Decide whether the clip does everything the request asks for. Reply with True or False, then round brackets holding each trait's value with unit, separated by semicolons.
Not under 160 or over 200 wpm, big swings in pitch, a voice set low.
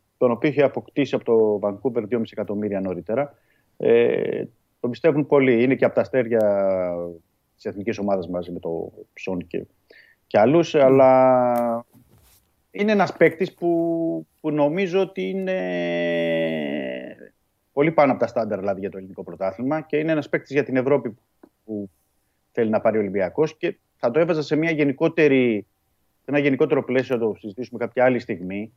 True (165 wpm; 6.9 semitones; 120 Hz)